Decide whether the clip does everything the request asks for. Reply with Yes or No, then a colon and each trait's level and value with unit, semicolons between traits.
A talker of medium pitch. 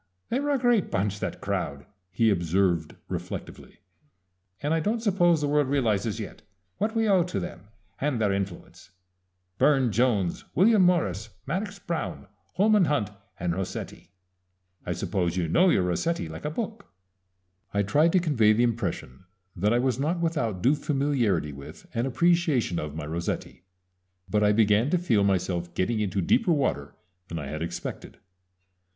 No: low, 115 Hz